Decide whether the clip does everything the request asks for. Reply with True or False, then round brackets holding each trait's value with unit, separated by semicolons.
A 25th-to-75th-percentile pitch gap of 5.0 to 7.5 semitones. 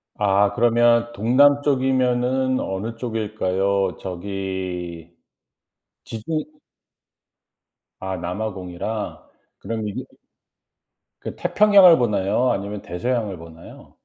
False (4.4 semitones)